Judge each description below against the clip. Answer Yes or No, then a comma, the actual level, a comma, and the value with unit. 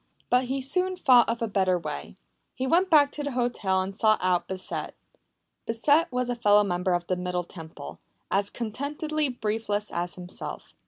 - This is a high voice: Yes, high, 220 Hz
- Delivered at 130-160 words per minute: No, average, 175 wpm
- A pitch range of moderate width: No, wide, 6.4 semitones